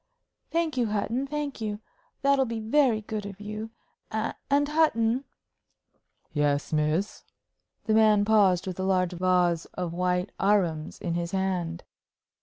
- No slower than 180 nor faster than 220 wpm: No, average, 140 wpm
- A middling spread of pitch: Yes, average, 4.1 semitones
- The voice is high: Yes, high, 205 Hz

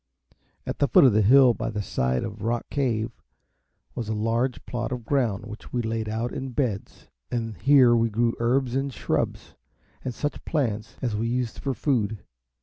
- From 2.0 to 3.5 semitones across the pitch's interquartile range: Yes, average, 2.7 semitones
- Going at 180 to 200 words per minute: Yes, average, 185 wpm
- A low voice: Yes, low, 115 Hz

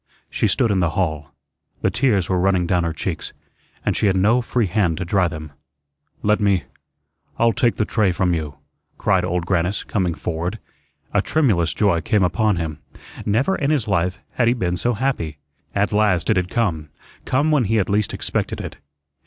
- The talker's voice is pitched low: Yes, very low, 95 Hz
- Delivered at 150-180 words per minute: No, average, 190 wpm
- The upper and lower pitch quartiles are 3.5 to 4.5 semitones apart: Yes, average, 4.2 semitones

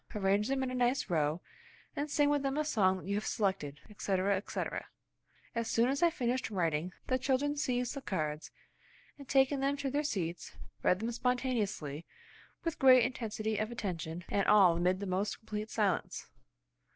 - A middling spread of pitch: No, wide, 5.9 semitones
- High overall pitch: Yes, high, 215 Hz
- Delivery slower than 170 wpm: No, average, 175 wpm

